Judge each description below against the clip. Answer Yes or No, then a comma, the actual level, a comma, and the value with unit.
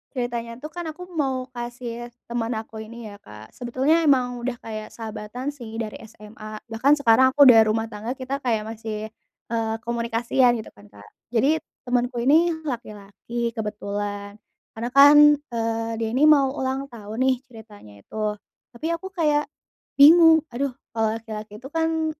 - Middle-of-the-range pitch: No, high, 235 Hz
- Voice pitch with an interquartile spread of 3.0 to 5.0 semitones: Yes, average, 3.6 semitones